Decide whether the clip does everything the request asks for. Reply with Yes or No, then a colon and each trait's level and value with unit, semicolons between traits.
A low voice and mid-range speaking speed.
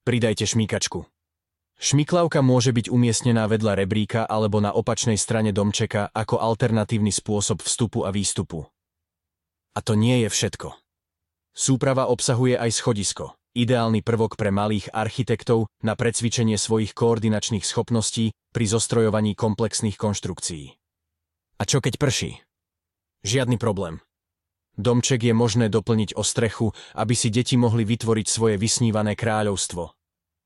Yes: low, 110 Hz; average, 120 wpm